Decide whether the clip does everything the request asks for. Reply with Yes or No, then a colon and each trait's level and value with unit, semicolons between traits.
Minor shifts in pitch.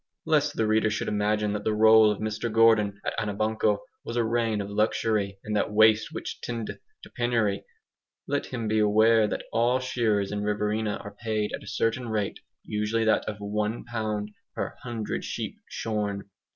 Yes: narrow, 1.4 semitones